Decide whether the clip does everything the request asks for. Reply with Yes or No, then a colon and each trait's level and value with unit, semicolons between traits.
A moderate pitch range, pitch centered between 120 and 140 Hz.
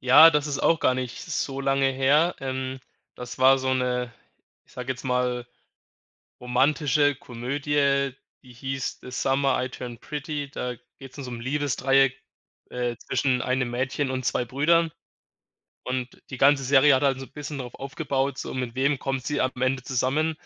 No: narrow, 1.8 semitones; low, 135 Hz